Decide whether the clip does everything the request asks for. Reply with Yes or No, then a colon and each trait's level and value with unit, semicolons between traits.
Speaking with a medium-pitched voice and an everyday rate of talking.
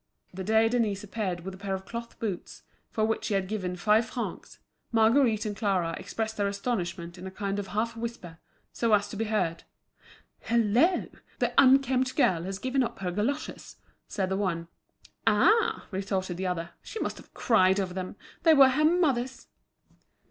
No: high, 210 Hz; average, 175 wpm